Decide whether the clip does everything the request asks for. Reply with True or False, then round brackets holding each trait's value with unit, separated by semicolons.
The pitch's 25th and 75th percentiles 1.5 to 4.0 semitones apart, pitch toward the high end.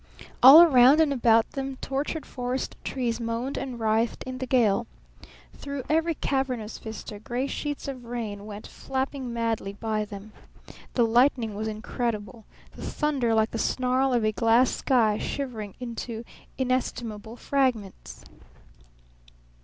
True (3.2 semitones; 240 Hz)